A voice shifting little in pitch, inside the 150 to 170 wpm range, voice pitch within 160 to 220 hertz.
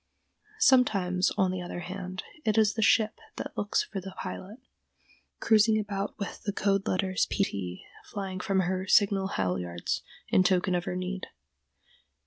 Yes: narrow, 2.1 semitones; average, 155 wpm; high, 190 Hz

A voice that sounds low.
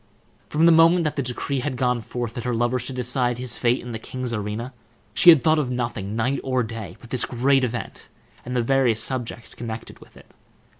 Yes: low, 125 Hz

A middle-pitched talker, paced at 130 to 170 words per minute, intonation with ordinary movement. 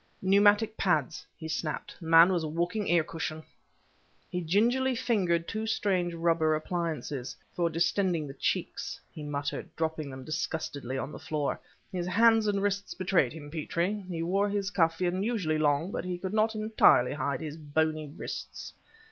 Yes: medium, 170 Hz; average, 165 wpm; average, 4.3 semitones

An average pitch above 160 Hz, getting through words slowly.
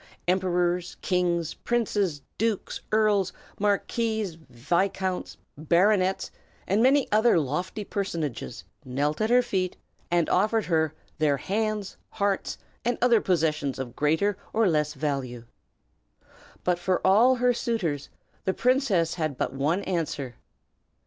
Yes: medium, 185 Hz; slow, 120 wpm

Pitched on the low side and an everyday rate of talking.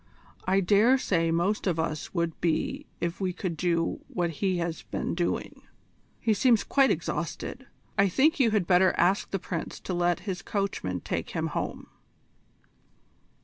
No: medium, 180 Hz; average, 160 wpm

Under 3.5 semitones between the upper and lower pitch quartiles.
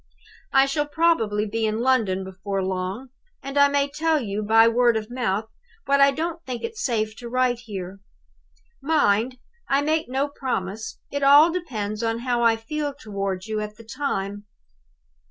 No: average, 5.0 semitones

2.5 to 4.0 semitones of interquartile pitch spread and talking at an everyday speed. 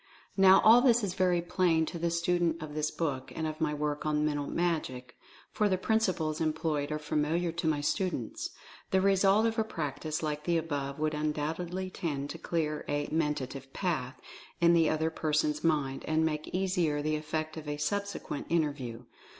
Yes: average, 2.8 semitones; average, 185 wpm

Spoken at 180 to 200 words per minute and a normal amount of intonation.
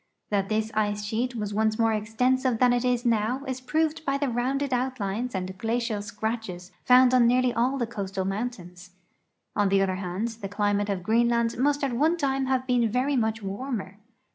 Yes: average, 190 wpm; average, 3.7 semitones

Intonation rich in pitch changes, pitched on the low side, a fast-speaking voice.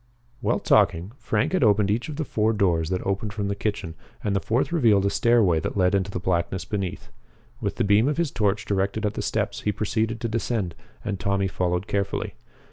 No: narrow, 2.6 semitones; low, 100 Hz; fast, 210 wpm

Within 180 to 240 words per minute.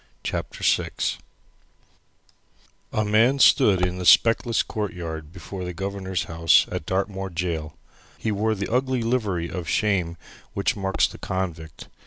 No: slow, 135 wpm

